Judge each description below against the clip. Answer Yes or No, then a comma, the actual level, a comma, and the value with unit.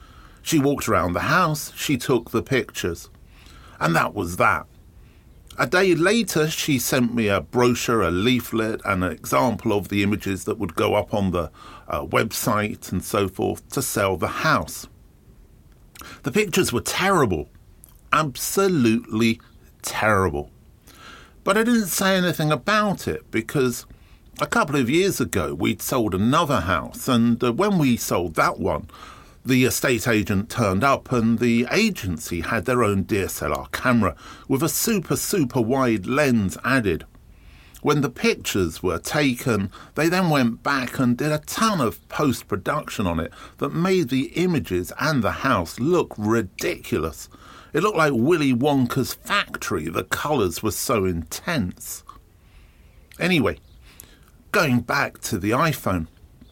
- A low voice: Yes, low, 115 Hz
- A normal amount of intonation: No, wide, 7.1 semitones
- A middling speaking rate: Yes, average, 145 wpm